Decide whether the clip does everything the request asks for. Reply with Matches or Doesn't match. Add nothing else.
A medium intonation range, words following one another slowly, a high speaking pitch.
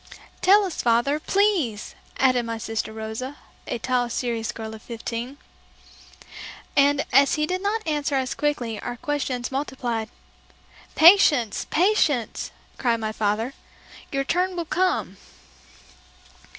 Matches